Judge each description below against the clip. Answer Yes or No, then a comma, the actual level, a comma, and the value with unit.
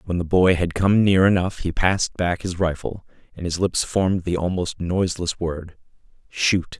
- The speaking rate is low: No, average, 185 wpm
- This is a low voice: Yes, very low, 90 Hz